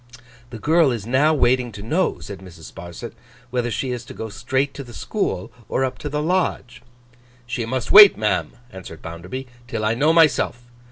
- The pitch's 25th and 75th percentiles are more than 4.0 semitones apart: Yes, average, 4.7 semitones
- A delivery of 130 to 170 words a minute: No, average, 185 wpm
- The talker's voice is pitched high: No, low, 125 Hz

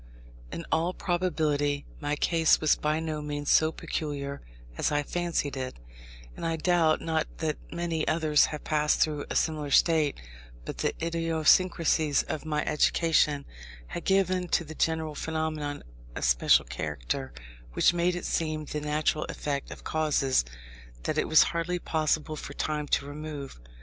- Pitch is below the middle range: No, medium, 155 Hz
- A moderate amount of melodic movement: No, narrow, 2.0 semitones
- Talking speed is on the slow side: No, average, 155 wpm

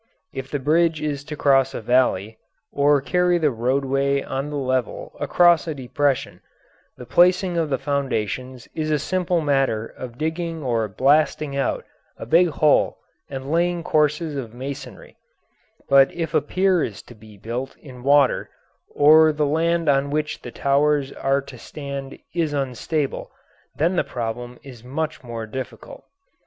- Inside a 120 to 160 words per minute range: Yes, average, 155 wpm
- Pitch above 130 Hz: Yes, medium, 140 Hz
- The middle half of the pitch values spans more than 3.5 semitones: No, average, 3.2 semitones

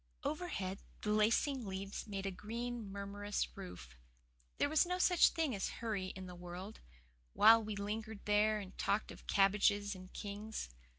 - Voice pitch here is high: Yes, high, 205 Hz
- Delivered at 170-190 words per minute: No, average, 160 wpm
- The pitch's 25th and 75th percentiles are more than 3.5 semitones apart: No, narrow, 2.4 semitones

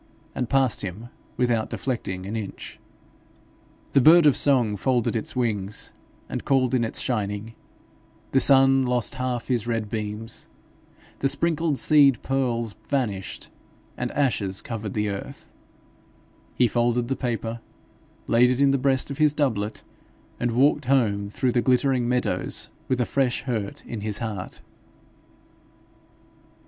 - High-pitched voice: No, low, 120 Hz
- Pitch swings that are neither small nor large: Yes, average, 3.6 semitones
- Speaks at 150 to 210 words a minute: No, average, 140 wpm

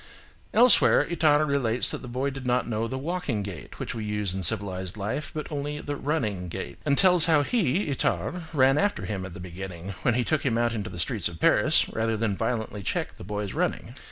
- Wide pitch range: Yes, wide, 6.4 semitones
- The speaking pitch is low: Yes, low, 120 Hz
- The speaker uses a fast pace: Yes, fast, 215 wpm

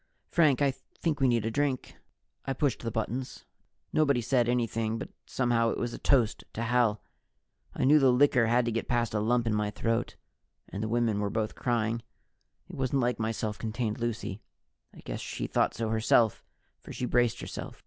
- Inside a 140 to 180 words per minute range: No, average, 195 wpm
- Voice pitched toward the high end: No, low, 120 Hz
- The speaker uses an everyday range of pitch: No, narrow, 2.2 semitones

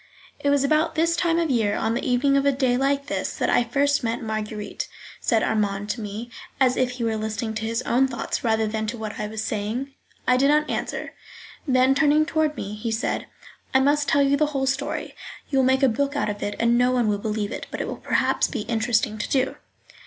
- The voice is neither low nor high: No, high, 245 Hz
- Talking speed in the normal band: No, fast, 235 wpm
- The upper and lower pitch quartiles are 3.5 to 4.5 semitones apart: Yes, average, 4.2 semitones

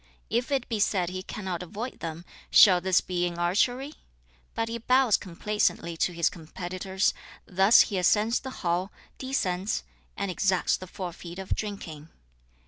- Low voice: No, high, 190 Hz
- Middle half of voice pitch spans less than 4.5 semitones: Yes, average, 3.6 semitones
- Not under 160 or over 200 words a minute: No, average, 150 wpm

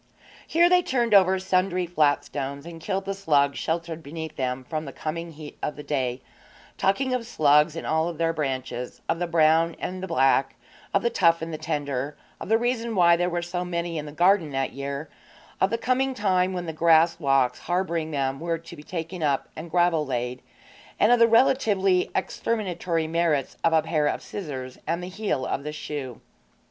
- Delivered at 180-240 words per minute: Yes, average, 200 wpm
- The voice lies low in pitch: No, medium, 165 Hz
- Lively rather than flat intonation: No, average, 3.9 semitones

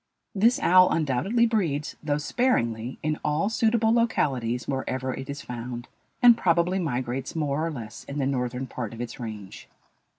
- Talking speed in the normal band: Yes, average, 160 wpm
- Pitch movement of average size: No, wide, 6.8 semitones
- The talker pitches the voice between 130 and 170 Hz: Yes, medium, 140 Hz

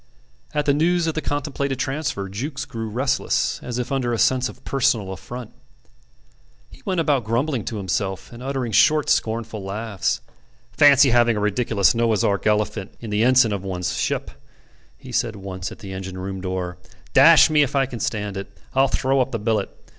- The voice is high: No, low, 115 Hz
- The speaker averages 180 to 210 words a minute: Yes, average, 185 wpm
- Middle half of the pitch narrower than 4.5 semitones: No, average, 5.1 semitones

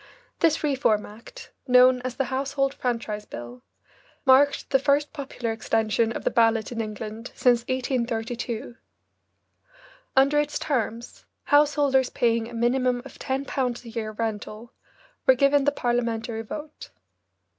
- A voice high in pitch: Yes, high, 245 Hz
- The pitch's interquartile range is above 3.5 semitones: No, average, 3.2 semitones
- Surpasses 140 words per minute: No, slow, 135 wpm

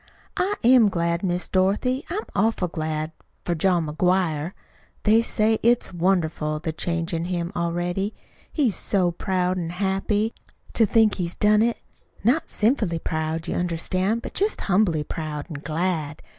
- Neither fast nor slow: Yes, average, 150 wpm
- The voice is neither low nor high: Yes, medium, 180 Hz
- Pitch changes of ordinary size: Yes, average, 4.3 semitones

